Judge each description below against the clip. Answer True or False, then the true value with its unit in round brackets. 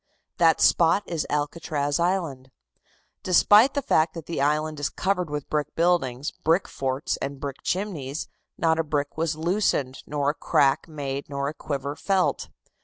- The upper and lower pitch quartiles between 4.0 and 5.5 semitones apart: False (3.2 semitones)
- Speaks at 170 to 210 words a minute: False (160 wpm)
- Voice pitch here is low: False (155 Hz)